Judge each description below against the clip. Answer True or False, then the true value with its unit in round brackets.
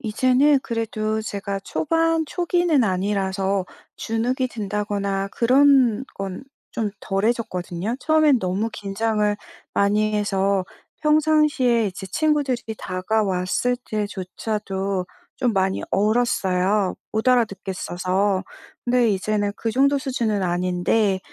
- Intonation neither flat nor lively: True (4.3 semitones)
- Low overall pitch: False (215 Hz)